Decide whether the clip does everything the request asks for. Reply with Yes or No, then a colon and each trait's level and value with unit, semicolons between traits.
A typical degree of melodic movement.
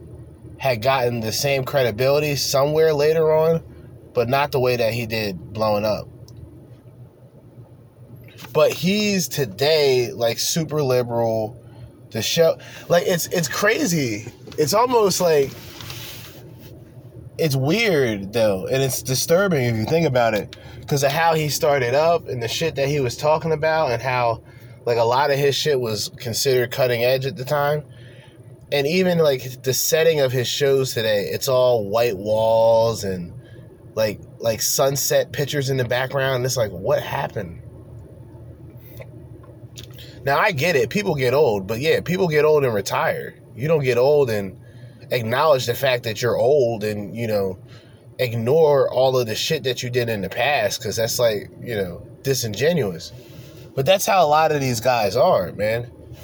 Yes: average, 3.4 semitones